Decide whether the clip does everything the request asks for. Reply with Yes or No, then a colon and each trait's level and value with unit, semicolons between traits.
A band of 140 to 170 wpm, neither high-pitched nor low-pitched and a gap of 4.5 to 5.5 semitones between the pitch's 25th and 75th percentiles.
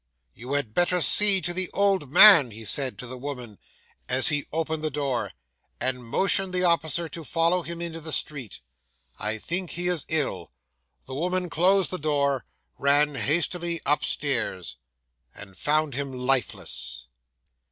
Yes: average, 150 wpm; medium, 150 Hz; average, 5.1 semitones